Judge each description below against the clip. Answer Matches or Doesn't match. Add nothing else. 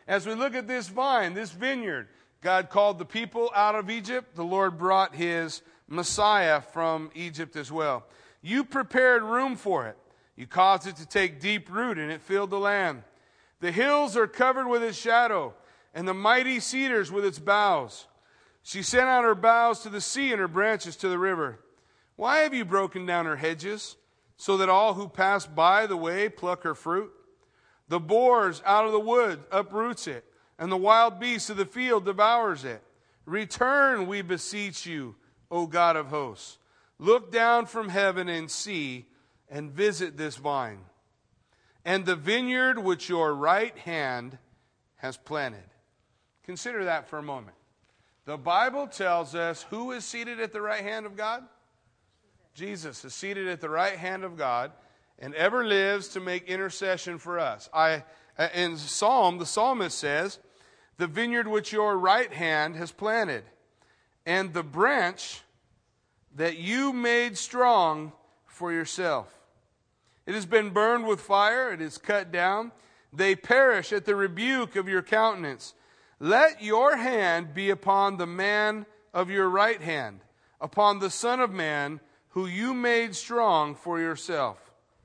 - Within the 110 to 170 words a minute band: Matches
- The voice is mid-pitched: Doesn't match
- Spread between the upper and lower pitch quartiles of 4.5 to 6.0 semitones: Matches